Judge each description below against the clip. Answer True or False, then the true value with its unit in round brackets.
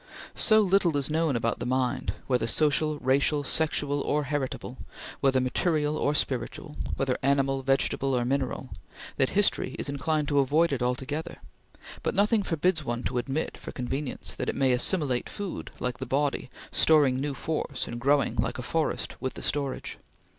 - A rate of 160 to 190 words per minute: True (170 wpm)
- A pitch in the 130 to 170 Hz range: True (140 Hz)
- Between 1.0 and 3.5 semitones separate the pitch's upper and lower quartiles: True (2.8 semitones)